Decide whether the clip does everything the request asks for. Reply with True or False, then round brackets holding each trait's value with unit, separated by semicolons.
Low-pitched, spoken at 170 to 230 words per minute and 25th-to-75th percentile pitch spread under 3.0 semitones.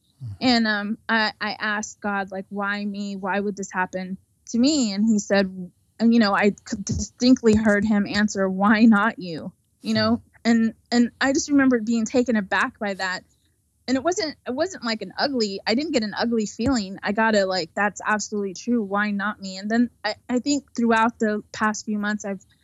False (215 Hz; 200 wpm; 2.6 semitones)